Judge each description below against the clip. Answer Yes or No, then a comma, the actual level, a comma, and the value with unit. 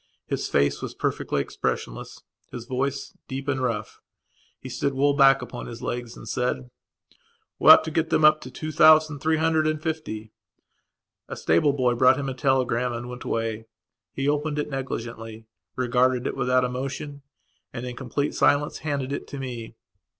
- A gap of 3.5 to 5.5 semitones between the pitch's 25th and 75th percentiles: No, average, 3.0 semitones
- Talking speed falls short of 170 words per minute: No, average, 175 wpm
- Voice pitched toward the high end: No, low, 130 Hz